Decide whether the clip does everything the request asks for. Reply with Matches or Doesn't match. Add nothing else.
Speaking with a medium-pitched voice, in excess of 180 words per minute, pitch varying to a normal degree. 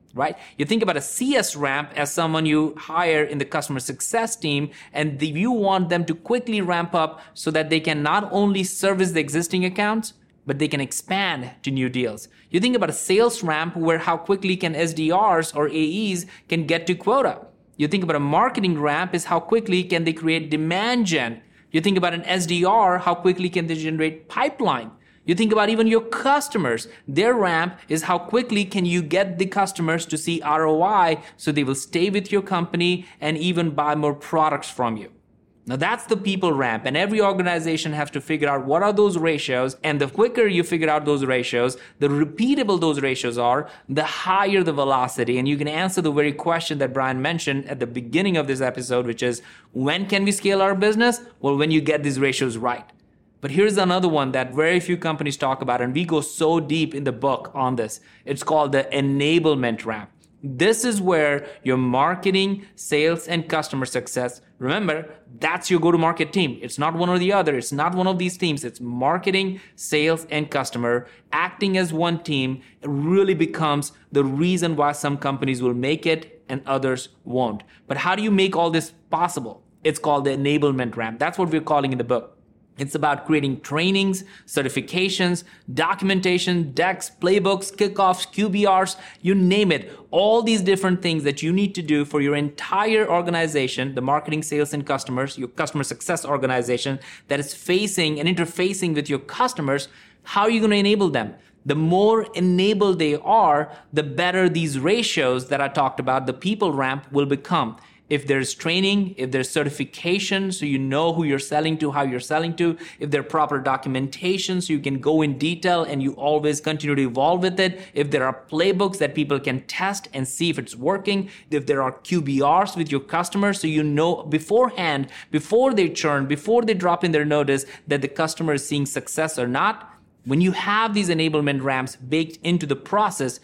Matches